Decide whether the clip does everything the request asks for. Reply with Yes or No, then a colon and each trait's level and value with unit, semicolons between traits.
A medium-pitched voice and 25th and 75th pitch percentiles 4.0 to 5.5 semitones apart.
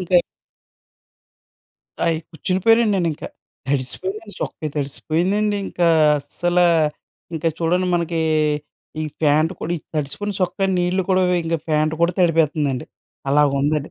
No: medium, 170 Hz; average, 3.4 semitones